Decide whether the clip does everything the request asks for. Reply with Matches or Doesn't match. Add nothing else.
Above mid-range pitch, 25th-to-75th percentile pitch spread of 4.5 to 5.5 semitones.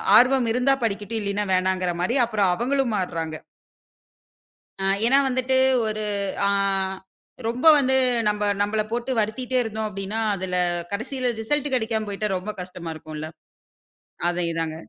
Matches